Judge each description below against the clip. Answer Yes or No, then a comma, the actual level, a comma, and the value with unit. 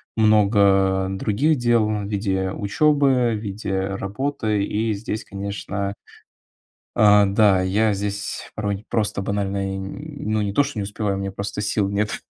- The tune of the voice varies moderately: No, narrow, 1.9 semitones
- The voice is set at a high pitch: No, low, 105 Hz